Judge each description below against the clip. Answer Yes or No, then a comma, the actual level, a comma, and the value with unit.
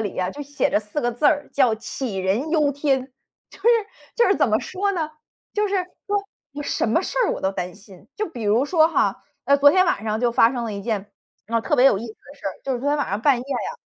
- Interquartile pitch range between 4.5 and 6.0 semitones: Yes, wide, 5.5 semitones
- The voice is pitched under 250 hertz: No, very high, 260 Hz